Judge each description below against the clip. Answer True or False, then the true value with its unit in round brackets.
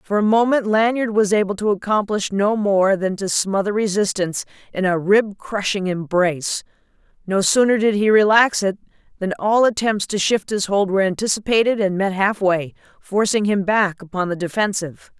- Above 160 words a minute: True (175 wpm)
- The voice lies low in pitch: False (200 Hz)